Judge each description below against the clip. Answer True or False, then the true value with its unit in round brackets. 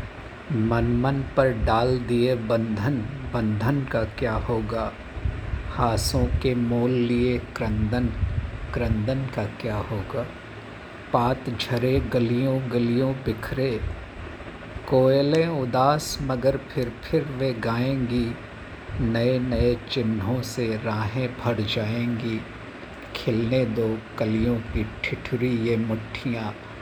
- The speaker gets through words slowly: True (100 wpm)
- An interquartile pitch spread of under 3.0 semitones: True (2.4 semitones)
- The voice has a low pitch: True (120 Hz)